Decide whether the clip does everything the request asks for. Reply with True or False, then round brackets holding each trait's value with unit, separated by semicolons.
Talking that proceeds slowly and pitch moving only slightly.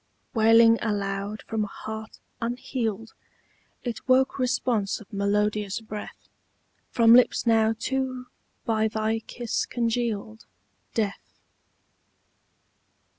True (95 wpm; 2.1 semitones)